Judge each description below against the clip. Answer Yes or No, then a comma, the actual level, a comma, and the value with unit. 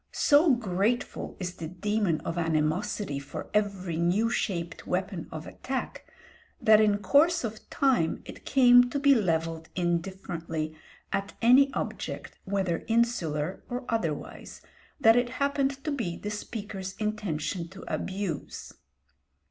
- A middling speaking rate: No, slow, 130 wpm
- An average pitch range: No, wide, 6.0 semitones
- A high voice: Yes, high, 200 Hz